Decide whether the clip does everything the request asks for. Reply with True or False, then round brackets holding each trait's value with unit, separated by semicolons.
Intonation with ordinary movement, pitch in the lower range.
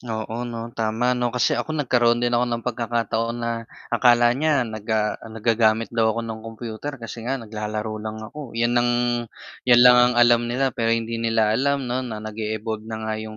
False (1.7 semitones; 115 Hz)